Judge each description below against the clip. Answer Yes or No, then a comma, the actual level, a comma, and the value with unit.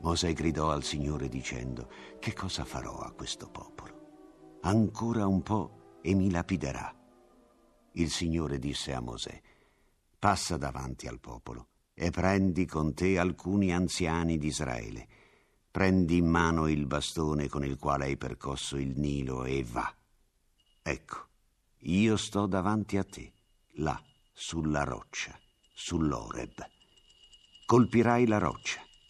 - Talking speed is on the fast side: No, average, 125 wpm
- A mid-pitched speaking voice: No, very low, 80 Hz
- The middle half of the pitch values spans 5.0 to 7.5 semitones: Yes, wide, 5.6 semitones